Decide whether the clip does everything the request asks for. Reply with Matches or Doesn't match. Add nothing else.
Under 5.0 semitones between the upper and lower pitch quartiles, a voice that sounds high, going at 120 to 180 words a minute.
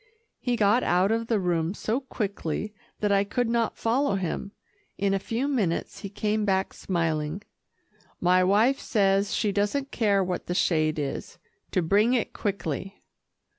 Matches